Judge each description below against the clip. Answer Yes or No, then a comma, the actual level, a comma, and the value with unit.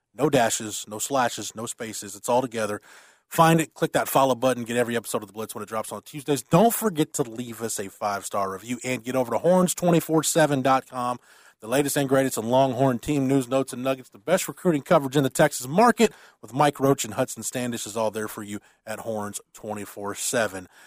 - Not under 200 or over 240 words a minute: Yes, fast, 205 wpm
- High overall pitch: No, low, 130 Hz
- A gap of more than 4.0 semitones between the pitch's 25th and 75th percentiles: Yes, average, 4.9 semitones